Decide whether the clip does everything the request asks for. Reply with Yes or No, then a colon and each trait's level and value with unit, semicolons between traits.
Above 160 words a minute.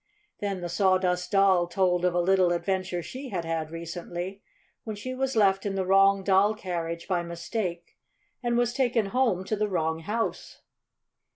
Yes: average, 170 wpm